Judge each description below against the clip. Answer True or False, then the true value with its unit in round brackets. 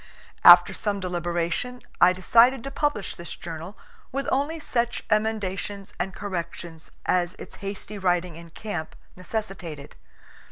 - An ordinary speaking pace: False (125 wpm)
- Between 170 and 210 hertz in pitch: True (190 Hz)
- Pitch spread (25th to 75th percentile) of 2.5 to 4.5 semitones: True (4.1 semitones)